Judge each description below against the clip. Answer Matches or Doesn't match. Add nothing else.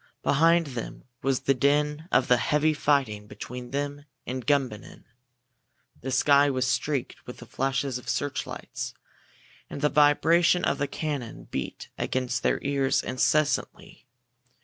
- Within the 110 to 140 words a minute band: Matches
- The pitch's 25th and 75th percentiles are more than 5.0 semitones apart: Doesn't match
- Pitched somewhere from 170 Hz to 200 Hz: Doesn't match